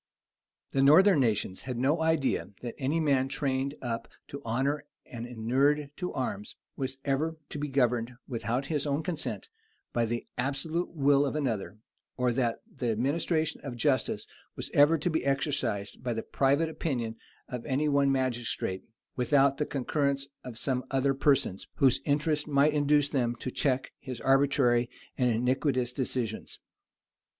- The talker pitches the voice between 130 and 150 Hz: Yes, low, 135 Hz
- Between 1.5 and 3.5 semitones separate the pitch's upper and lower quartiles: Yes, average, 2.9 semitones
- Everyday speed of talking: Yes, average, 155 wpm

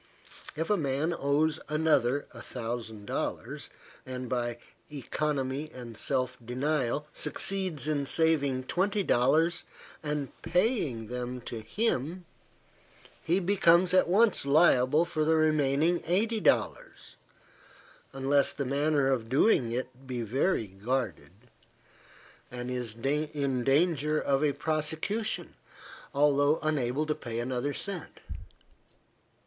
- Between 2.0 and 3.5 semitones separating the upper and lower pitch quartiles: No, average, 4.0 semitones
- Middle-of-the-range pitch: Yes, medium, 145 Hz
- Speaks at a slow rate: Yes, slow, 115 wpm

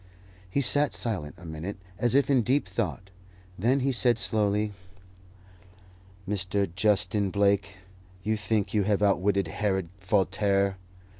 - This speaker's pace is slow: Yes, slow, 130 wpm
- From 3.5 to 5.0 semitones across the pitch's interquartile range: No, narrow, 2.5 semitones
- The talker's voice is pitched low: Yes, low, 100 Hz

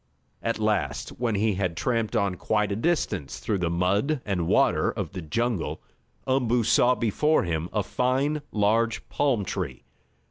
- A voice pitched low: Yes, low, 110 Hz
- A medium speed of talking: Yes, average, 155 wpm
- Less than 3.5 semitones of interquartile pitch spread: No, average, 4.5 semitones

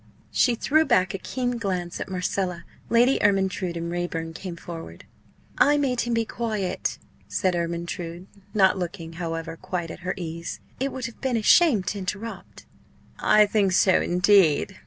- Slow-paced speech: No, average, 160 wpm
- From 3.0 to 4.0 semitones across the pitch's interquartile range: No, average, 4.7 semitones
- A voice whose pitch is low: No, medium, 185 Hz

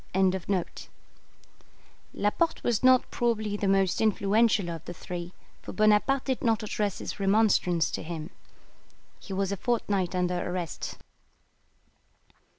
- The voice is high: Yes, high, 200 Hz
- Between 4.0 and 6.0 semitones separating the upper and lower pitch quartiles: No, average, 3.5 semitones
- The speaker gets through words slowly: Yes, slow, 125 wpm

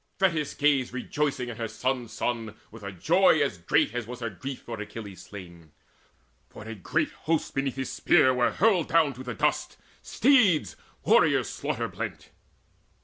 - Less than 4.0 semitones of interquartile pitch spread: No, wide, 5.5 semitones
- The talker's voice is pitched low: Yes, low, 125 Hz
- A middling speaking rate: Yes, average, 165 wpm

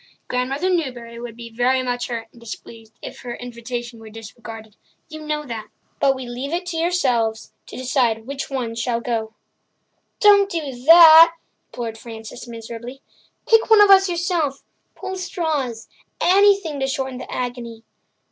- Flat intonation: No, wide, 5.6 semitones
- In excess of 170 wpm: No, average, 145 wpm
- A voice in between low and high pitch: No, very high, 250 Hz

